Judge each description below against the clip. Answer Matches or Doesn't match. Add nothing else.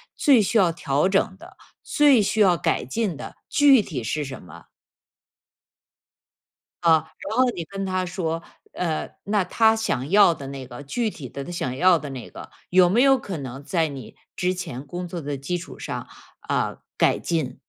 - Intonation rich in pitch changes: Matches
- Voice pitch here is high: Doesn't match